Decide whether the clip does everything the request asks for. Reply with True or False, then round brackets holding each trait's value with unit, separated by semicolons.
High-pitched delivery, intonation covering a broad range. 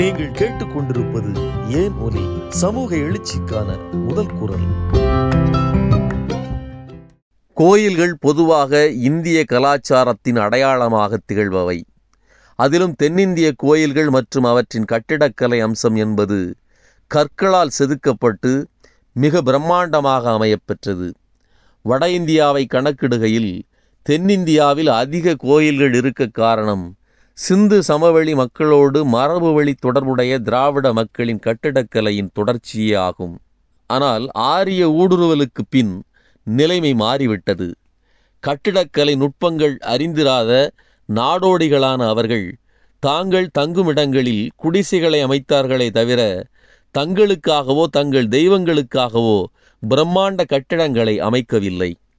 False (130 Hz; 5.7 semitones)